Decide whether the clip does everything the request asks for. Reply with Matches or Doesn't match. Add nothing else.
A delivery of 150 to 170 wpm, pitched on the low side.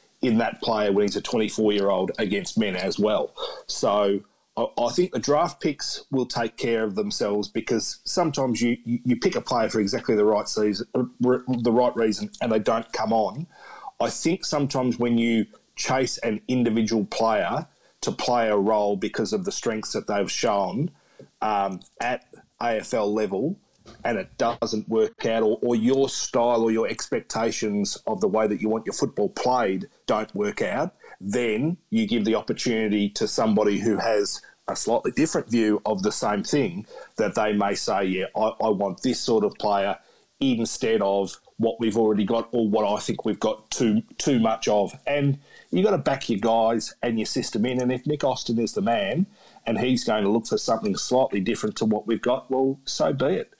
Doesn't match